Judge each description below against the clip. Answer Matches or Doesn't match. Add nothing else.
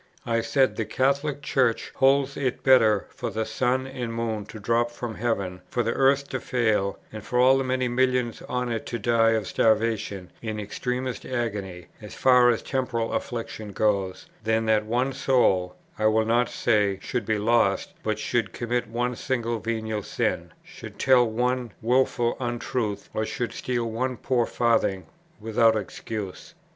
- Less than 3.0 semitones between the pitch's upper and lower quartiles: Matches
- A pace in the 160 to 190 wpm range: Matches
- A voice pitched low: Matches